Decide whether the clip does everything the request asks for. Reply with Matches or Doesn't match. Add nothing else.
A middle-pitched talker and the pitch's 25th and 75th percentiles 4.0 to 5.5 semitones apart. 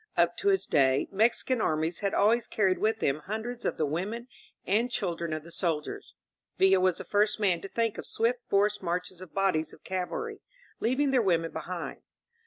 Doesn't match